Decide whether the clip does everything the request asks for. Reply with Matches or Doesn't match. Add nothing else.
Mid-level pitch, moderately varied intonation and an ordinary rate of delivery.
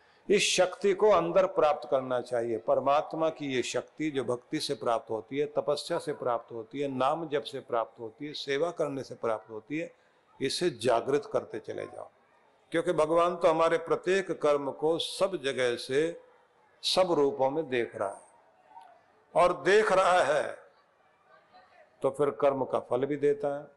Matches